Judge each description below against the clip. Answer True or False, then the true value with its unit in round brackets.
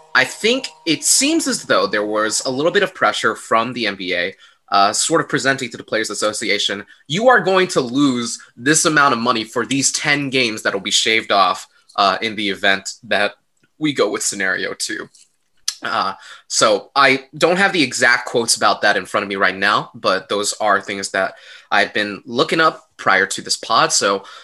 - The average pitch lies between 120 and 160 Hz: True (135 Hz)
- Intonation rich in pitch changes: True (6.8 semitones)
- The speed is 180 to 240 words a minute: True (200 wpm)